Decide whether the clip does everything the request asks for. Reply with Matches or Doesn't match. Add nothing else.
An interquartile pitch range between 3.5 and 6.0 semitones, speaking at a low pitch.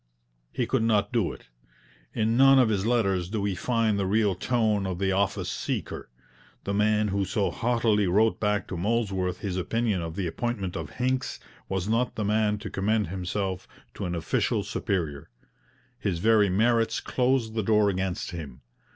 Doesn't match